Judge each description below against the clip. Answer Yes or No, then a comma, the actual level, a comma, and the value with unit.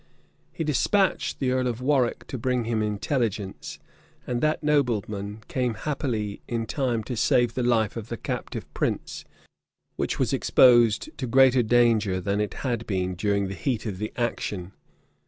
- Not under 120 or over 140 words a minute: No, average, 160 wpm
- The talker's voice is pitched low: Yes, low, 115 Hz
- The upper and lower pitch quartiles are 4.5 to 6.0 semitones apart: No, average, 3.3 semitones